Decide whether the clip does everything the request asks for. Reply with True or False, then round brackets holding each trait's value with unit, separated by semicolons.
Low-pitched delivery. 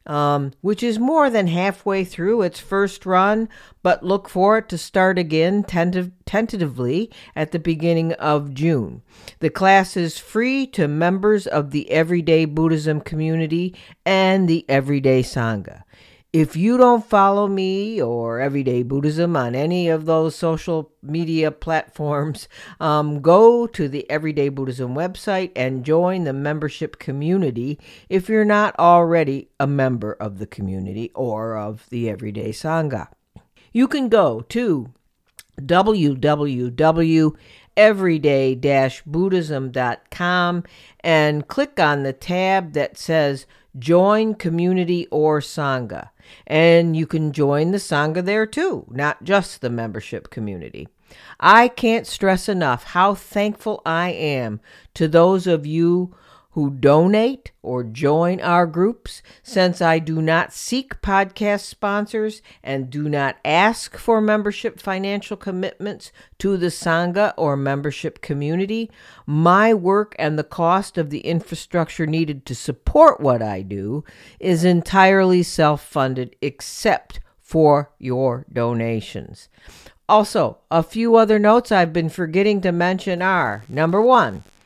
False (165 Hz)